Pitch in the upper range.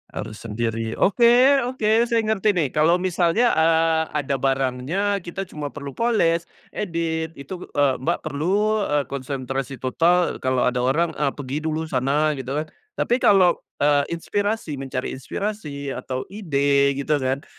No: medium, 155 Hz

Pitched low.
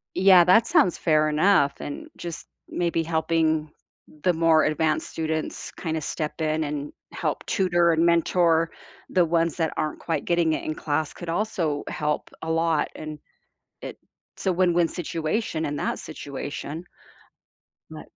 No: medium, 160 Hz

